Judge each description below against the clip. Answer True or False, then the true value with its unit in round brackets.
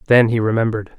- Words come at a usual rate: True (180 wpm)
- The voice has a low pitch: True (110 Hz)